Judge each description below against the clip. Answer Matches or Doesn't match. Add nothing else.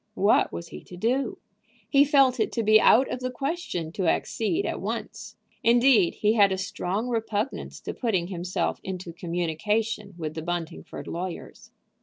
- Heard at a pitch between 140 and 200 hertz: Doesn't match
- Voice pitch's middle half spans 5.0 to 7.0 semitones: Matches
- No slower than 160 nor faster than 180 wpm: Matches